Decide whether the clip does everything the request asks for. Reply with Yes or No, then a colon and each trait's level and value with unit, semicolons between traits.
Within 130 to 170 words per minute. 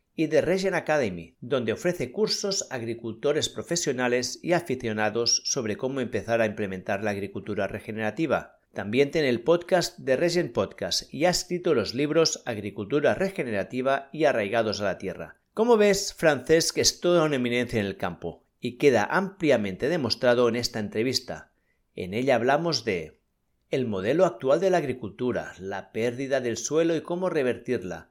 Yes: average, 155 wpm